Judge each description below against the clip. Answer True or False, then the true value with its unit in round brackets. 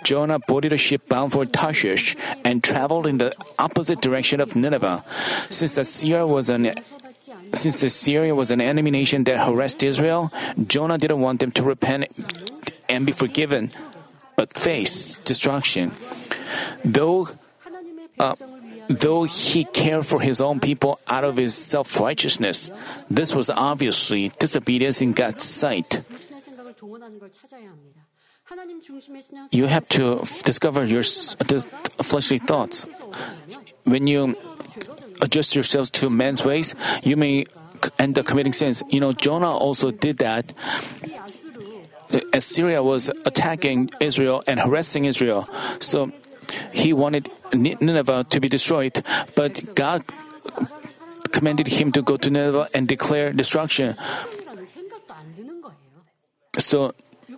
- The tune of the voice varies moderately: True (4.2 semitones)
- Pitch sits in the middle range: True (145 Hz)